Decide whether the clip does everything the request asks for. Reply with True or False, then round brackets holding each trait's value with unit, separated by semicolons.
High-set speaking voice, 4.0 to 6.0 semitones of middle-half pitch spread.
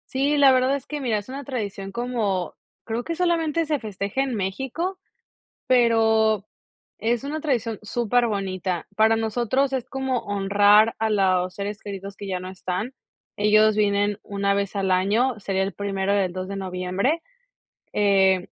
True (215 Hz; 4.4 semitones)